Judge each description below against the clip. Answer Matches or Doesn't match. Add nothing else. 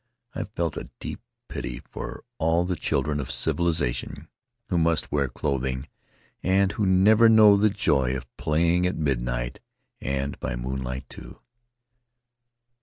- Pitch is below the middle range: Matches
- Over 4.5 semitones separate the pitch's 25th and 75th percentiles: Matches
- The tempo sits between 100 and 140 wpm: Matches